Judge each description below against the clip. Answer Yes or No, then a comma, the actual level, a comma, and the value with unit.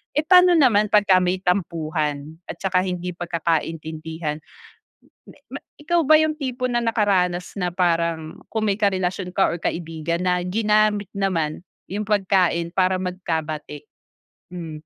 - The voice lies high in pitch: No, medium, 180 Hz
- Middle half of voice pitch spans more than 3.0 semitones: Yes, average, 3.8 semitones